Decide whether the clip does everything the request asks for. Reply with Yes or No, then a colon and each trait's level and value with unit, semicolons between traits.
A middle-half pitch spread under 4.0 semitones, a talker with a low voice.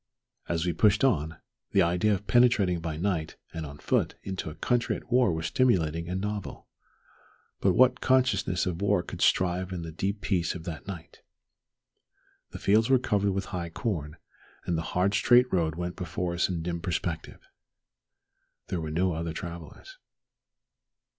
Yes: average, 3.5 semitones; very low, 90 Hz